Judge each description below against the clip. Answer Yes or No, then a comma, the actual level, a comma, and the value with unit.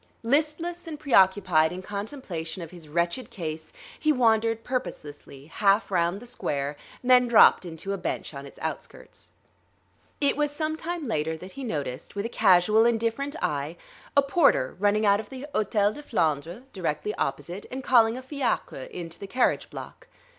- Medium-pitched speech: No, high, 205 Hz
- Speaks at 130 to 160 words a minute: No, average, 170 wpm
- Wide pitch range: Yes, wide, 7.4 semitones